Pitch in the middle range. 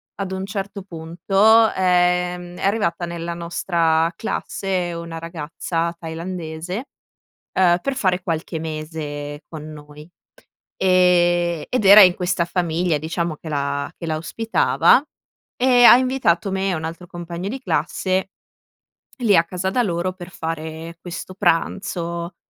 Yes: medium, 175 Hz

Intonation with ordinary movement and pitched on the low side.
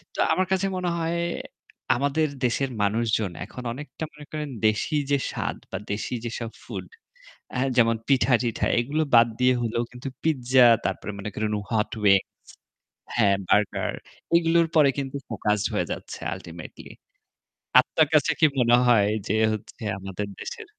No: wide, 5.7 semitones; low, 120 Hz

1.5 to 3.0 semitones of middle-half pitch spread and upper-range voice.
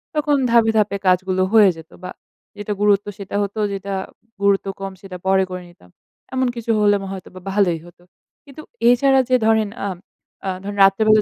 Yes: narrow, 2.5 semitones; high, 200 Hz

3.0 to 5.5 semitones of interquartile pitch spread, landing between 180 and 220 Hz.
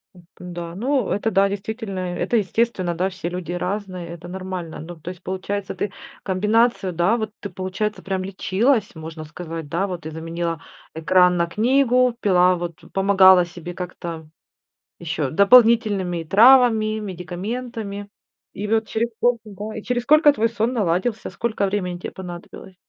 Yes: average, 3.8 semitones; high, 190 Hz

